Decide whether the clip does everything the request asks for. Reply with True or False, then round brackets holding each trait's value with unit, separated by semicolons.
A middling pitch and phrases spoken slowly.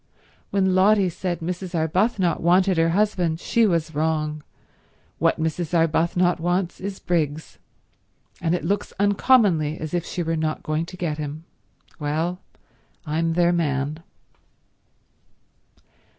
True (170 Hz; 125 wpm)